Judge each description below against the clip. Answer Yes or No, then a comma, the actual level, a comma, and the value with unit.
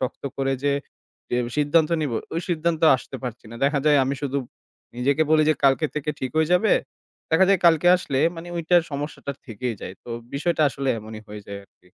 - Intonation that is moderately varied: Yes, average, 3.9 semitones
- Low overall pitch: No, medium, 145 Hz